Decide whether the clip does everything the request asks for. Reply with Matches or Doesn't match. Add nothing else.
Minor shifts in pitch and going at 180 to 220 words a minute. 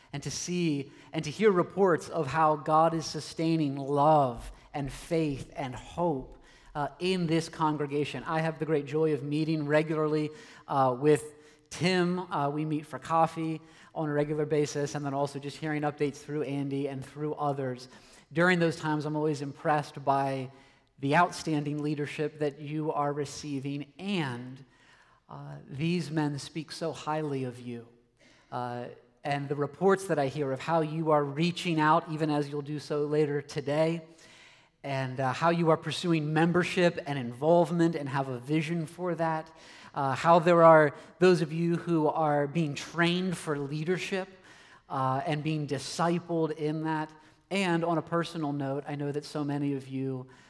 Doesn't match